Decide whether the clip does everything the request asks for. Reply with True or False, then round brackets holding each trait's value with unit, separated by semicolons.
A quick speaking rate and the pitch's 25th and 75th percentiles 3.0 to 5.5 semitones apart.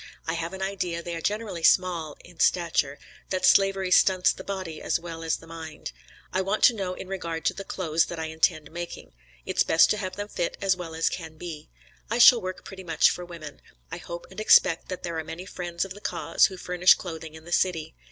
False (220 wpm; 2.5 semitones)